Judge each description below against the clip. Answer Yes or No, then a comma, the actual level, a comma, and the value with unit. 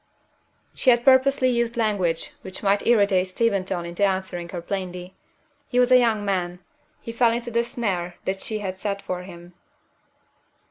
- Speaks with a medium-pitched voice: No, high, 200 Hz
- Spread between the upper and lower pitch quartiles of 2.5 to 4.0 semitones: No, average, 4.4 semitones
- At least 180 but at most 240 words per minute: No, average, 165 wpm